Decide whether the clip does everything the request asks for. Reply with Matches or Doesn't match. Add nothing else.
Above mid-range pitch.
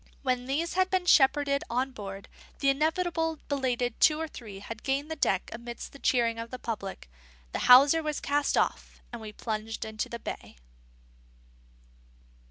Matches